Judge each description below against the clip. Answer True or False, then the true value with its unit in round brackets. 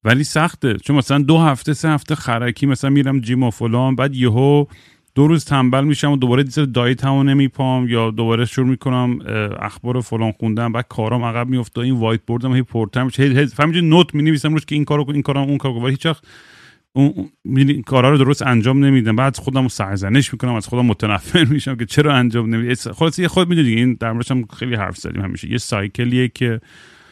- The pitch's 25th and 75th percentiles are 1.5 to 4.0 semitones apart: True (3.2 semitones)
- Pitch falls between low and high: False (130 Hz)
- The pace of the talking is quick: True (200 wpm)